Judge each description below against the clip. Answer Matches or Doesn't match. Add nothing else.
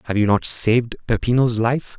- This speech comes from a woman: Doesn't match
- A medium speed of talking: Matches